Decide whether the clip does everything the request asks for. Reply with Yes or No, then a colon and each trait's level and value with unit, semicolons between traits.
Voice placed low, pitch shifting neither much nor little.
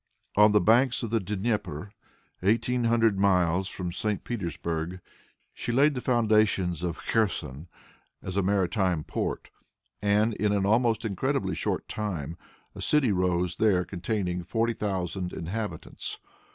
Yes: low, 100 Hz; average, 3.8 semitones